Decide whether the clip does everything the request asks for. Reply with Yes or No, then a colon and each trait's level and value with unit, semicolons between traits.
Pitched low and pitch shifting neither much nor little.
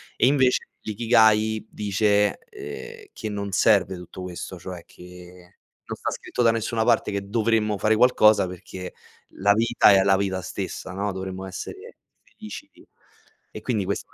Yes: low, 105 Hz; average, 3.1 semitones